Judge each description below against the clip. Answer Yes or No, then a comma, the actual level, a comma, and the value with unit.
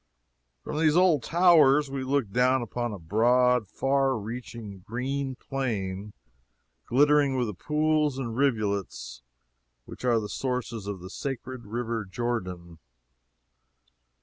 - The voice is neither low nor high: No, low, 125 Hz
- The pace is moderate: No, slow, 120 wpm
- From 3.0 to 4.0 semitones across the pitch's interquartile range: No, average, 4.5 semitones